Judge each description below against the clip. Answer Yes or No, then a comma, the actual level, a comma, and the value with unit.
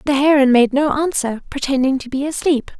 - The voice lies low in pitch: No, very high, 275 Hz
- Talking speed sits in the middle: No, fast, 215 wpm